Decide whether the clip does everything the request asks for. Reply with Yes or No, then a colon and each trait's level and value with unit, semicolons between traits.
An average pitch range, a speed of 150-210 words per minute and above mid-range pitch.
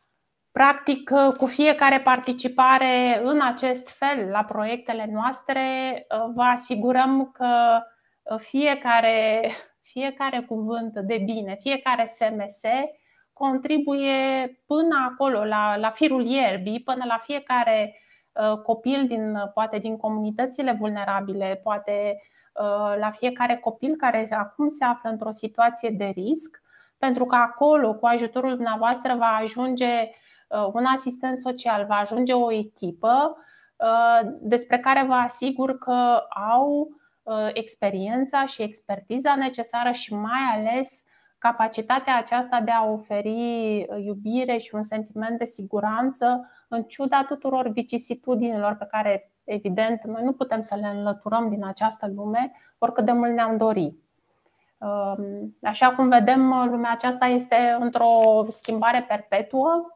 No: average, 3.1 semitones; slow, 115 wpm; high, 235 Hz